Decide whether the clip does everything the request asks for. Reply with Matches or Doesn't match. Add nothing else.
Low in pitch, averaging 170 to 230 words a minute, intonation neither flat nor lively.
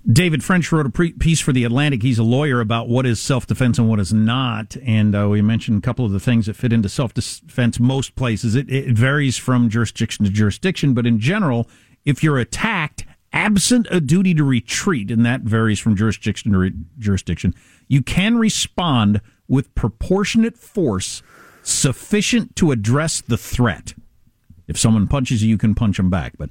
Matches